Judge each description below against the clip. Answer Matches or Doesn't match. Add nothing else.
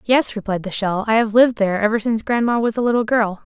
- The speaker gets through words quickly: Matches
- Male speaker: Doesn't match